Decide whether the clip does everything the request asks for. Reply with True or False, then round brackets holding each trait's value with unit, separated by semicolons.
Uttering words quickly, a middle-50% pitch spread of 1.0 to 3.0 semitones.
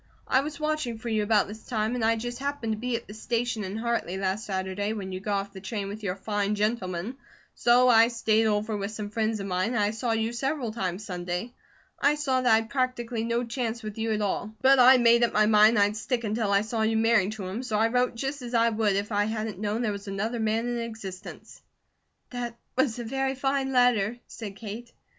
True (230 wpm; 2.6 semitones)